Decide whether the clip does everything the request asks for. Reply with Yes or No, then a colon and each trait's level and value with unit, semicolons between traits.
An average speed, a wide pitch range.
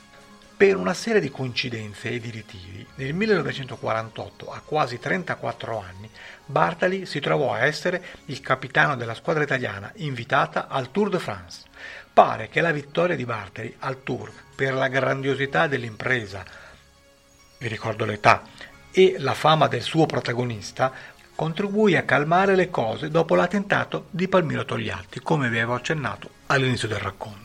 Yes: average, 145 wpm; wide, 6.4 semitones